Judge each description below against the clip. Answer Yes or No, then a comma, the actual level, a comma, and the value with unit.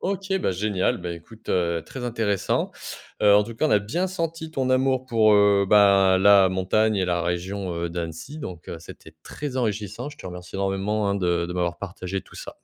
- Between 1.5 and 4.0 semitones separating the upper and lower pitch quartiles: No, average, 4.6 semitones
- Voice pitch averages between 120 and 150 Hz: No, low, 100 Hz